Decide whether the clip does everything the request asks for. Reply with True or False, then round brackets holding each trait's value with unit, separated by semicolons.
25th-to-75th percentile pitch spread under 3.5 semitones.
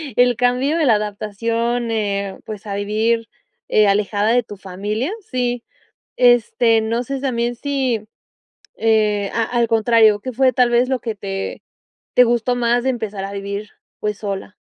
True (2.8 semitones)